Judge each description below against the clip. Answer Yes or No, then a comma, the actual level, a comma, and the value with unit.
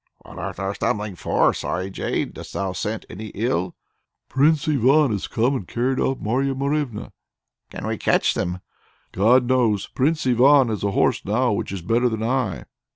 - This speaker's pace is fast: No, average, 175 wpm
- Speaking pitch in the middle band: No, low, 115 Hz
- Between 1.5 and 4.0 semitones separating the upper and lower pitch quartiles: No, average, 4.6 semitones